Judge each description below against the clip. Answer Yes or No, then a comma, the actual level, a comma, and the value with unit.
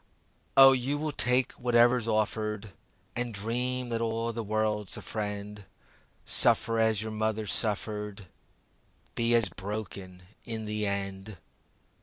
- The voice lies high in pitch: No, low, 110 Hz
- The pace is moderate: No, slow, 125 wpm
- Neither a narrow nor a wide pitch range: No, narrow, 2.1 semitones